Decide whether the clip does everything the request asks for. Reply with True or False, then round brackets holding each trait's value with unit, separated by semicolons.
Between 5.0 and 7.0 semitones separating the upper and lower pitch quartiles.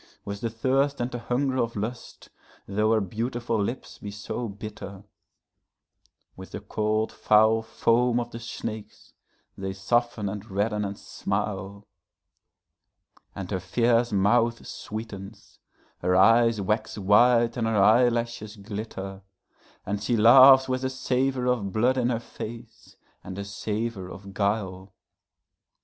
False (3.0 semitones)